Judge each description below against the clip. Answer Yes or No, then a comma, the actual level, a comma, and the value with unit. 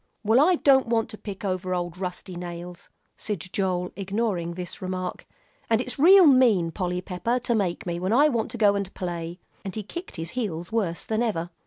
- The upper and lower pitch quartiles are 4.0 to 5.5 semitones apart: Yes, average, 4.4 semitones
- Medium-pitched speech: No, high, 195 Hz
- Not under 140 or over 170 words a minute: No, average, 200 wpm